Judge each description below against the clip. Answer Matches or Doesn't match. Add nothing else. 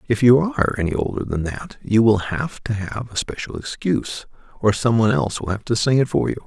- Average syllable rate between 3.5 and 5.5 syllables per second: Doesn't match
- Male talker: Matches